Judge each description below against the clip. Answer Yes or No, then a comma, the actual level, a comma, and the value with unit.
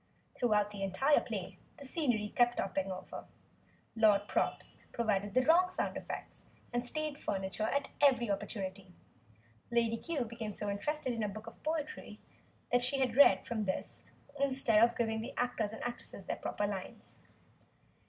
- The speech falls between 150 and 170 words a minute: Yes, average, 160 wpm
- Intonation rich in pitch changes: No, average, 4.0 semitones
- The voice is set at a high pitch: Yes, high, 230 Hz